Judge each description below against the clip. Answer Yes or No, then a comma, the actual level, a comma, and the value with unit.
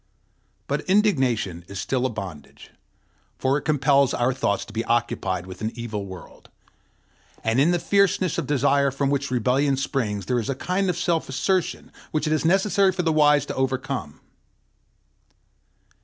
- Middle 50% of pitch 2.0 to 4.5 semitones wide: No, average, 5.2 semitones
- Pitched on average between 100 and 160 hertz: Yes, low, 135 Hz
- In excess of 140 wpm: Yes, average, 165 wpm